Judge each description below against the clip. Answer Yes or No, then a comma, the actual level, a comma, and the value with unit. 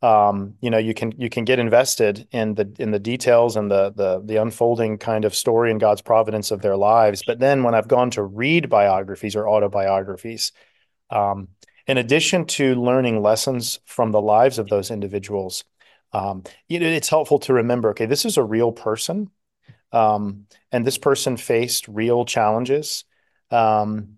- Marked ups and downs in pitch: No, average, 3.0 semitones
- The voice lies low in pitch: Yes, low, 115 Hz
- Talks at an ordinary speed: Yes, average, 180 wpm